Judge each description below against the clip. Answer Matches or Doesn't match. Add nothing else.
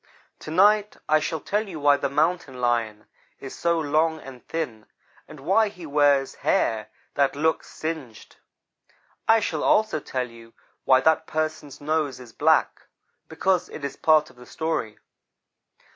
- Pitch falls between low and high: Matches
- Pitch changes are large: Doesn't match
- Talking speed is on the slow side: Doesn't match